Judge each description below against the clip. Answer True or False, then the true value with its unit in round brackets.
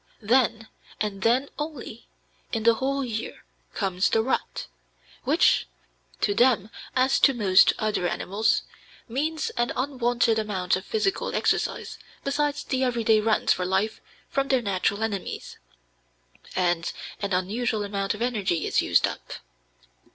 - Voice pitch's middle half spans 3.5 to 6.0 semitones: True (4.3 semitones)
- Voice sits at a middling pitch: False (225 Hz)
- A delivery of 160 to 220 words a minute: False (135 wpm)